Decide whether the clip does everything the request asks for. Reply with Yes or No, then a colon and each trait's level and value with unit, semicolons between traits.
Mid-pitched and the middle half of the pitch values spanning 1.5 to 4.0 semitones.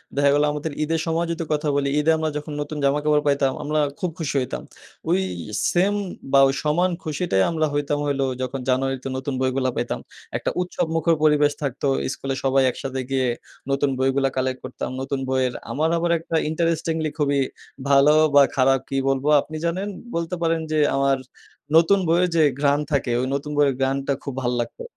Yes: medium, 145 Hz; average, 3.1 semitones